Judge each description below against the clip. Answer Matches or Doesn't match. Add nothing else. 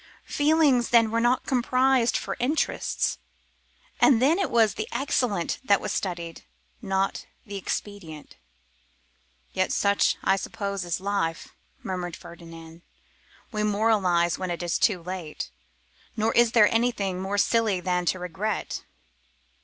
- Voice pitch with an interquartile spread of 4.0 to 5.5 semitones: Matches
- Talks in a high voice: Matches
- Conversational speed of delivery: Doesn't match